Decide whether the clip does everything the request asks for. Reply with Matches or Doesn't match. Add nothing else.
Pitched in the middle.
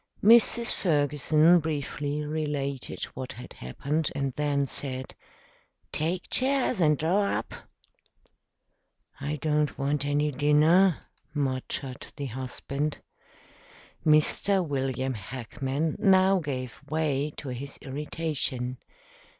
Matches